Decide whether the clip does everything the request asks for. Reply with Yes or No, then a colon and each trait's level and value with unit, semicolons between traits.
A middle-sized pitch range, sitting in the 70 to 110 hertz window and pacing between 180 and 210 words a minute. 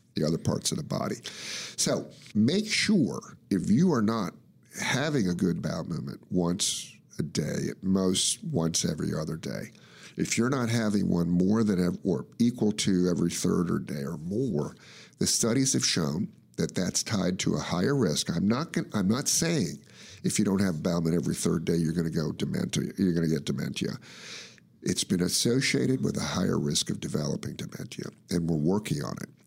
Yes: average, 3.2 semitones; very low, 90 Hz; average, 195 wpm